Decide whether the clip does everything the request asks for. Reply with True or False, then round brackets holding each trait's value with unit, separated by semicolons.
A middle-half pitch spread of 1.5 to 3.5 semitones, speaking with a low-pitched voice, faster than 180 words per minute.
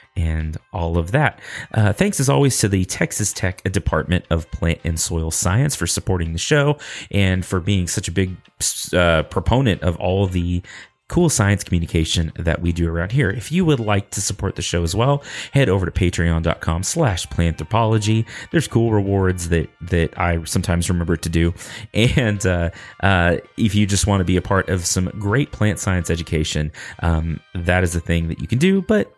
False (4.0 semitones; 95 Hz; 195 wpm)